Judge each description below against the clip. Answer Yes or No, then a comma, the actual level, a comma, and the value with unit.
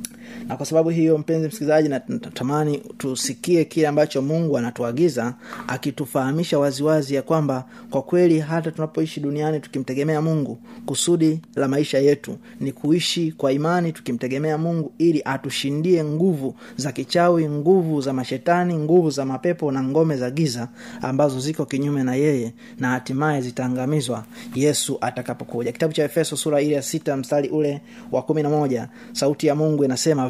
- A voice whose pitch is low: No, medium, 150 Hz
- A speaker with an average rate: No, fast, 145 wpm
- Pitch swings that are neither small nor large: Yes, average, 3.0 semitones